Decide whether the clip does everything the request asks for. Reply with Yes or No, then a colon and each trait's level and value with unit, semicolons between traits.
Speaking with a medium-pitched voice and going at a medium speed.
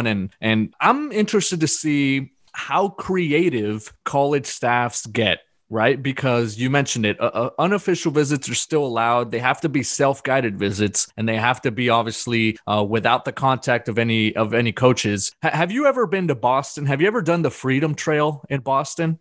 No: low, 130 Hz; average, 185 wpm